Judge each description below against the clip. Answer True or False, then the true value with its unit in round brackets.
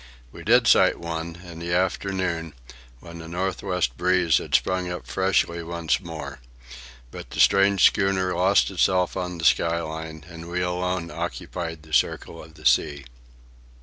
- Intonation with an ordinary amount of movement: False (2.0 semitones)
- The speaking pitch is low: True (85 Hz)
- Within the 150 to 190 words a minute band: True (160 wpm)